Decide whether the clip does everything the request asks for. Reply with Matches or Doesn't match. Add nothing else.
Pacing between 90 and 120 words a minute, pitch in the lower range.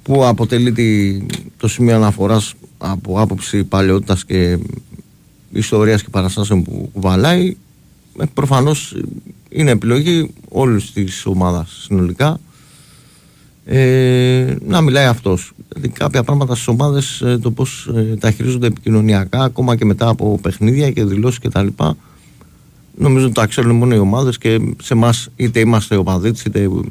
Doesn't match